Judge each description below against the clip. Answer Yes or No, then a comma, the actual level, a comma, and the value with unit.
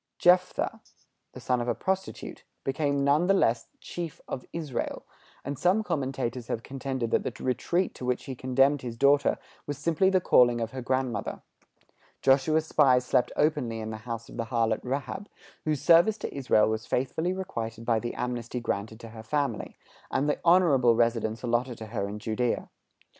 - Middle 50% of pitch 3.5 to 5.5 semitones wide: Yes, average, 4.3 semitones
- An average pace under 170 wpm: No, average, 175 wpm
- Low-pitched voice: Yes, low, 130 Hz